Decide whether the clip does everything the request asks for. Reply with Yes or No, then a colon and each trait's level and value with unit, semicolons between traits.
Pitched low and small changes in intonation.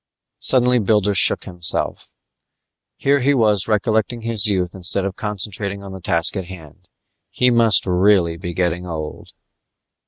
No: low, 100 Hz; average, 3.7 semitones